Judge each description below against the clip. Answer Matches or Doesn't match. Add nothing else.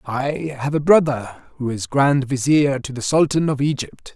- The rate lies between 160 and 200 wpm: Matches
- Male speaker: Matches